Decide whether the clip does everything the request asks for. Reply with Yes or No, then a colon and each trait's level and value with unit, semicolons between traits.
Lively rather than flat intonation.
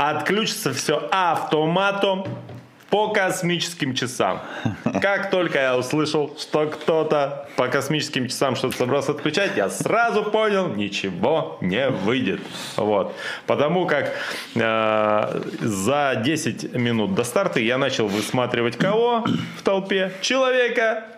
Yes: wide, 7.6 semitones